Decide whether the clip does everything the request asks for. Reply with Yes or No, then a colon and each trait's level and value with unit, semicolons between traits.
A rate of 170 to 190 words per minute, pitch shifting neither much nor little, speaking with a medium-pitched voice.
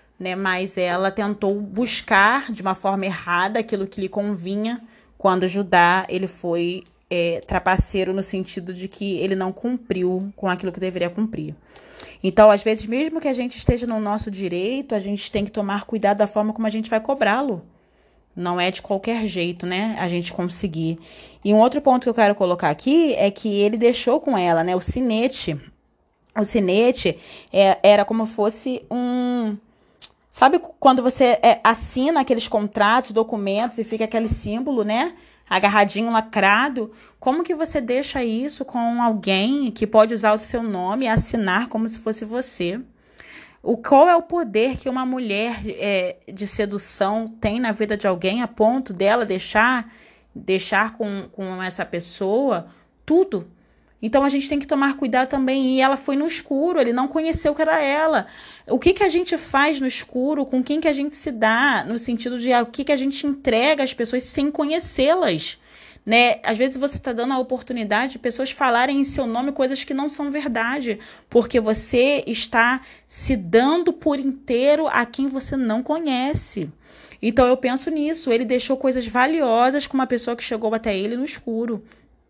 No: average, 180 wpm; average, 4.6 semitones; high, 230 Hz